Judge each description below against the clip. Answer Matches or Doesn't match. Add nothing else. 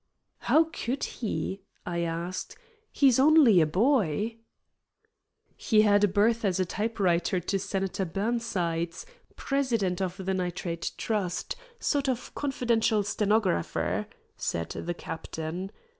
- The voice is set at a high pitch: Matches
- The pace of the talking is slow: Matches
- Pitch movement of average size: Matches